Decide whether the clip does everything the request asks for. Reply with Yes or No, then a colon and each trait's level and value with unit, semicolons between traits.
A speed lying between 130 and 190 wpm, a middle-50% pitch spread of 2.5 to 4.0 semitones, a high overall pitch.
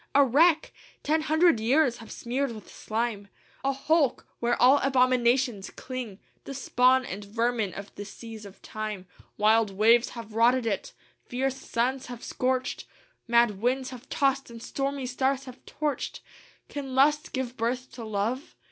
Yes: average, 155 wpm; average, 3.0 semitones; very high, 250 Hz